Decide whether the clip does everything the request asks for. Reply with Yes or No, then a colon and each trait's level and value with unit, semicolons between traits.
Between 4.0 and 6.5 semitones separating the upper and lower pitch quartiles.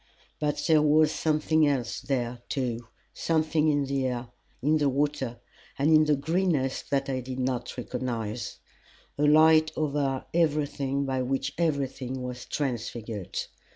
No: average, 3.2 semitones